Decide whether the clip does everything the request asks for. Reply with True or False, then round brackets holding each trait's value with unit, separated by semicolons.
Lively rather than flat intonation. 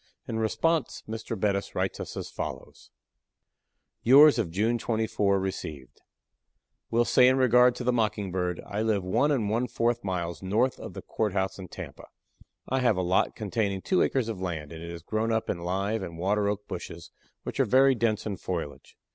False (4.1 semitones)